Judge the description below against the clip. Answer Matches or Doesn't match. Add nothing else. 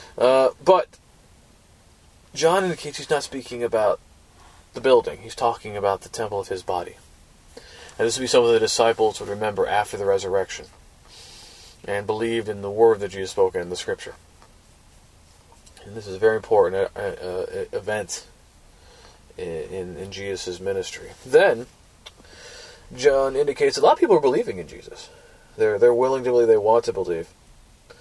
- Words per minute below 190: Matches